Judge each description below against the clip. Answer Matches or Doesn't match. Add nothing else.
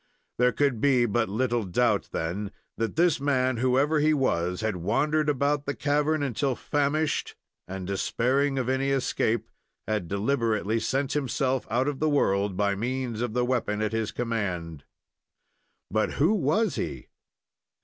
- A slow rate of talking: Doesn't match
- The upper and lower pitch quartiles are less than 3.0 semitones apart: Doesn't match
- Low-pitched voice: Matches